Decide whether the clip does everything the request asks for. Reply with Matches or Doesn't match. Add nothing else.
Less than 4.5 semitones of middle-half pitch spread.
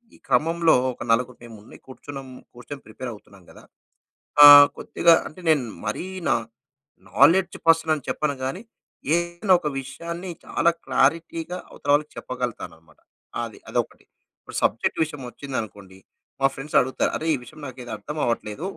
Doesn't match